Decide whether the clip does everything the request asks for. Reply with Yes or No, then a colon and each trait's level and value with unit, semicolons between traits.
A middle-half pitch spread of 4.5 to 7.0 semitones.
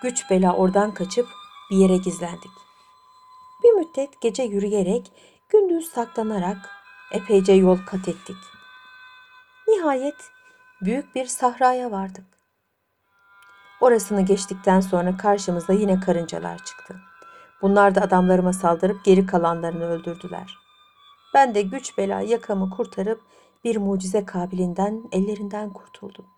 Yes: average, 5.3 semitones